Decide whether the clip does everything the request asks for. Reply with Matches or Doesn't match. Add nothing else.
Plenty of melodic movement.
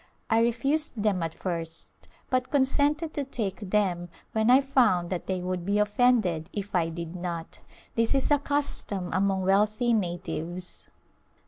Matches